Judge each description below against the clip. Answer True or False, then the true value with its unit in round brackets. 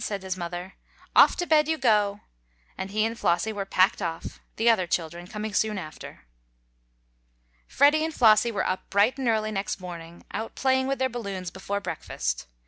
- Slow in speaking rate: False (180 wpm)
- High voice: True (205 Hz)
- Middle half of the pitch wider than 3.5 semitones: True (4.1 semitones)